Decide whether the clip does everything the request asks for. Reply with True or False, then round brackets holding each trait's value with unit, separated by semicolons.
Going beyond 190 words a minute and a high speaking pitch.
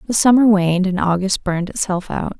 True (200 wpm; 195 Hz)